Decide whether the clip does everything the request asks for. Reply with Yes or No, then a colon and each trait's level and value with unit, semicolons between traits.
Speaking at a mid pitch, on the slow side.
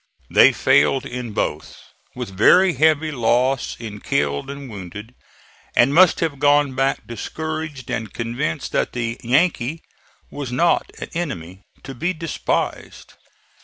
No: low, 130 Hz; slow, 130 wpm